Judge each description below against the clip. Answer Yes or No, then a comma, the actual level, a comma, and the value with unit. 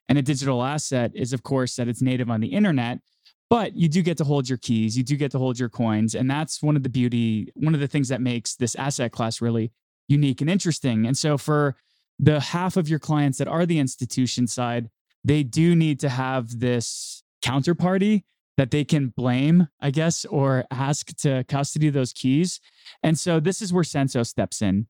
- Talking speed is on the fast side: Yes, fast, 210 wpm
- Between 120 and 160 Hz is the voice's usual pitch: Yes, low, 135 Hz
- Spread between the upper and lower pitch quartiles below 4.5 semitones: Yes, average, 3.6 semitones